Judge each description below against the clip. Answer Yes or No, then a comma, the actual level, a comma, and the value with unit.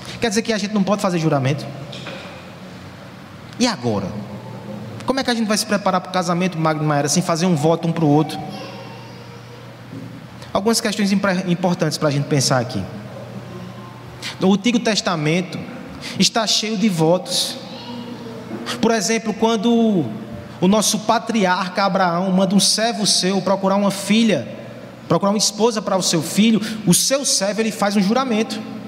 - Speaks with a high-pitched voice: Yes, high, 195 Hz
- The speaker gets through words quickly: No, average, 155 wpm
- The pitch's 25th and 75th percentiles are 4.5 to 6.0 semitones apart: Yes, average, 4.9 semitones